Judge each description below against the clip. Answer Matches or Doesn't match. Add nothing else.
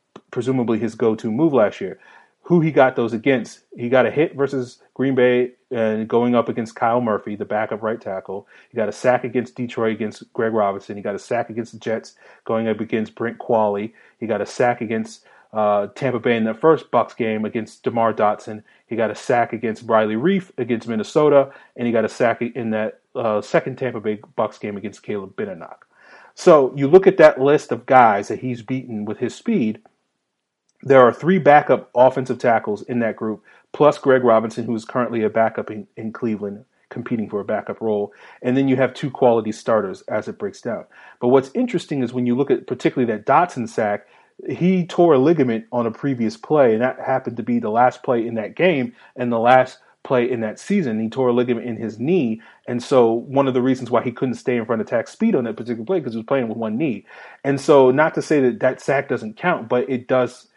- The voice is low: Matches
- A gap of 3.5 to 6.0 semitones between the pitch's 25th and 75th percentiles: Doesn't match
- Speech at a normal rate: Doesn't match